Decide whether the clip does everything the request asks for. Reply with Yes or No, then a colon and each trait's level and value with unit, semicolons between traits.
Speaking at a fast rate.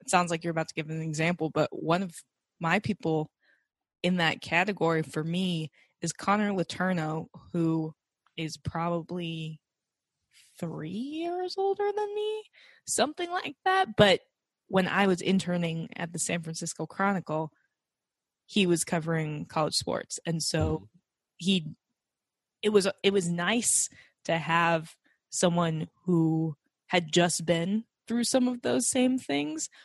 No: average, 140 wpm